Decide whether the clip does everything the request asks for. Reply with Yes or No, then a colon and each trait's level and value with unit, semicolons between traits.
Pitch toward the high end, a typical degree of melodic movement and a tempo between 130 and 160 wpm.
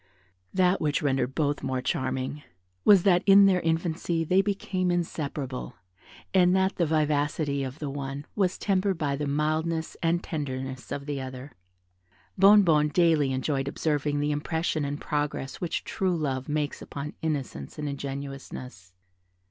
No: medium, 150 Hz; average, 3.7 semitones; average, 145 wpm